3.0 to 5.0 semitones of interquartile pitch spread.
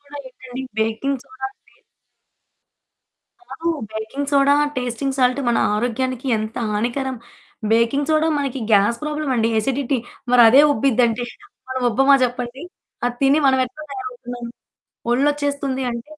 No: narrow, 2.6 semitones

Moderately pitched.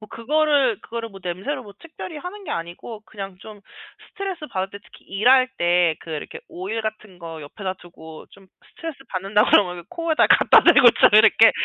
No: high, 210 Hz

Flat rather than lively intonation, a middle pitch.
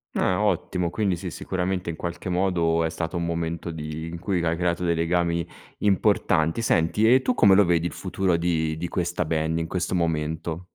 No: narrow, 2.0 semitones; very low, 85 Hz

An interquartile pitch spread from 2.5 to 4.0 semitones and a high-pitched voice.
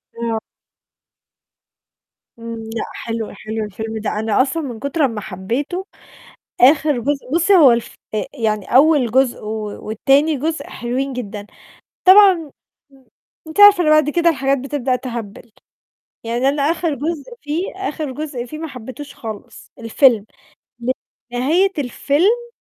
No: average, 5.2 semitones; very high, 270 Hz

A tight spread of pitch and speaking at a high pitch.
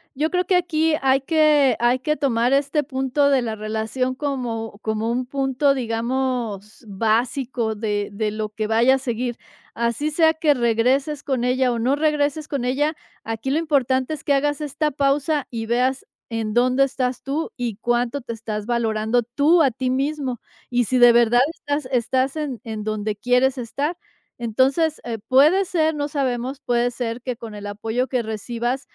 No: average, 3.5 semitones; very high, 255 Hz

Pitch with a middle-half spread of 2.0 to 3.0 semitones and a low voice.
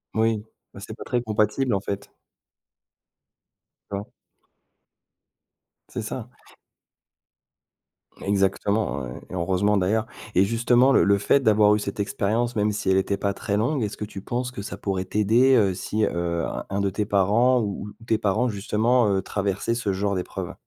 Yes: narrow, 2.4 semitones; low, 105 Hz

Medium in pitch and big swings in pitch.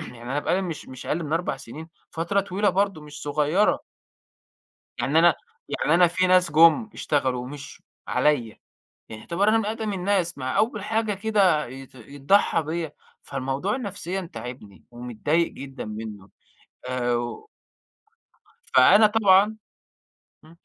Yes: medium, 165 Hz; wide, 6.5 semitones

